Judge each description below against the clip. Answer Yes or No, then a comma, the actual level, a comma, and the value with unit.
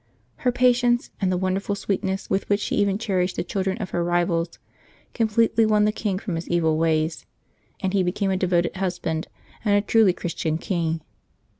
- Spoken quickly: No, average, 185 wpm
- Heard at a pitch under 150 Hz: No, high, 190 Hz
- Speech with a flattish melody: No, average, 3.2 semitones